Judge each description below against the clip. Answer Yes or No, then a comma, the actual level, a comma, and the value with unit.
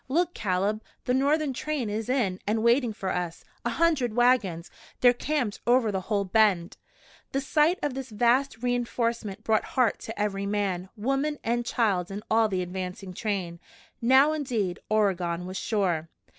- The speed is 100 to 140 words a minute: No, average, 165 wpm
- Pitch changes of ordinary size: Yes, average, 4.8 semitones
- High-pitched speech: Yes, high, 220 Hz